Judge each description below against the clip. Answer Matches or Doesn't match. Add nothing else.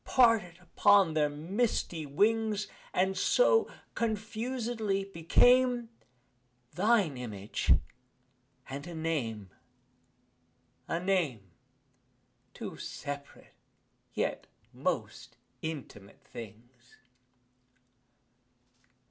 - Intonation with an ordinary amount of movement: Doesn't match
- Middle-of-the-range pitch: Matches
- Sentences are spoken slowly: Matches